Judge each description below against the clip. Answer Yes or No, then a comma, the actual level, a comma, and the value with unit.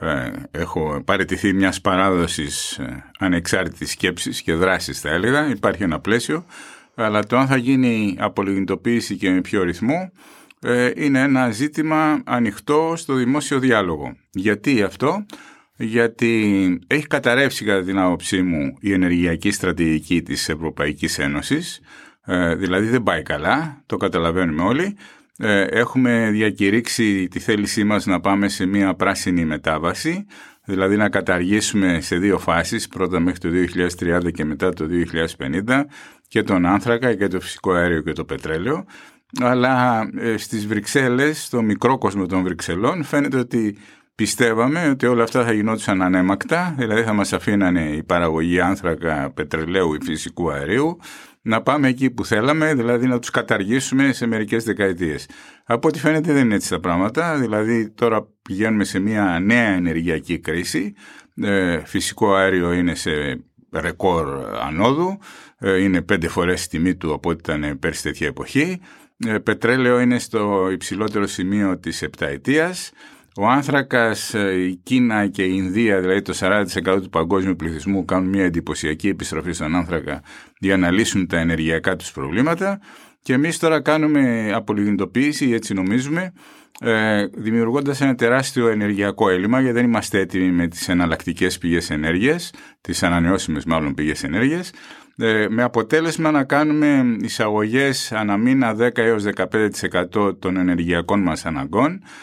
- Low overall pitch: Yes, low, 100 Hz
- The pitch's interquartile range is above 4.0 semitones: Yes, average, 5.1 semitones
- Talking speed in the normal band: Yes, average, 140 wpm